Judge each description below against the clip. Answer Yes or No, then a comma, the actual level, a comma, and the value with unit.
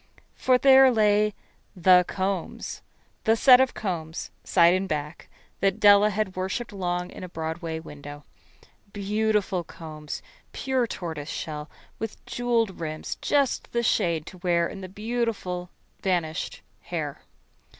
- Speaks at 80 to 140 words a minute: Yes, slow, 135 wpm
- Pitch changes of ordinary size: Yes, average, 4.5 semitones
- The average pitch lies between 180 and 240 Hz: Yes, medium, 185 Hz